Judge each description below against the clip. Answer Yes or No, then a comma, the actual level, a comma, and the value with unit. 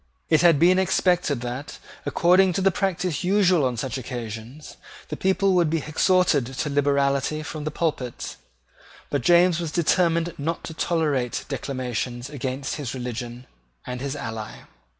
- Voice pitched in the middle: Yes, medium, 150 Hz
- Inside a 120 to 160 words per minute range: Yes, average, 150 wpm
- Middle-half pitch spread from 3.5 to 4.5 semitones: No, average, 5.2 semitones